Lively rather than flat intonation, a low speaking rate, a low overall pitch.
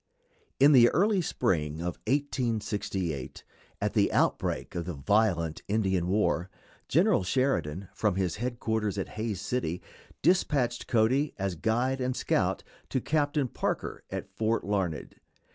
Yes: wide, 5.9 semitones; slow, 125 wpm; low, 110 Hz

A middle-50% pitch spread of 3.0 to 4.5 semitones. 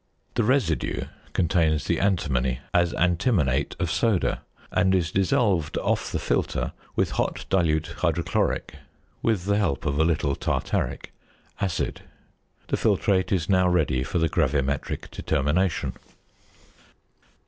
Yes: average, 3.7 semitones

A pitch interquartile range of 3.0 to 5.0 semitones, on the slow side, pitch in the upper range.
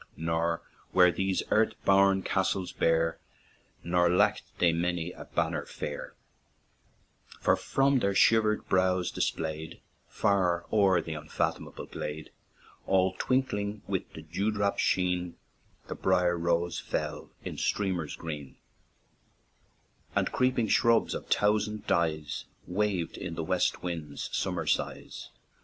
No: average, 3.4 semitones; slow, 120 wpm; very low, 90 Hz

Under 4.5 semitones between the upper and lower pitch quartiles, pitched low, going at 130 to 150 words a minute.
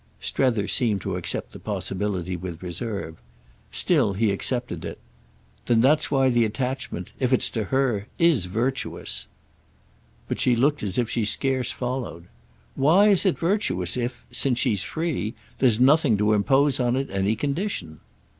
No: average, 5.0 semitones; low, 120 Hz; average, 140 wpm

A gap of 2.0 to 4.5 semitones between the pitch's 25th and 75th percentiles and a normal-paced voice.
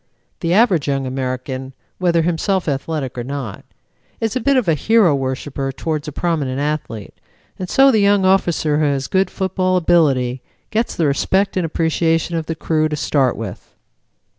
No: average, 5.2 semitones; average, 170 wpm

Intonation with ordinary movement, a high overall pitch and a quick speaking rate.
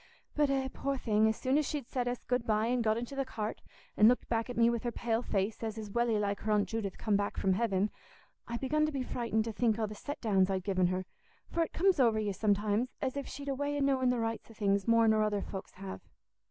Yes: average, 3.5 semitones; high, 225 Hz; fast, 265 wpm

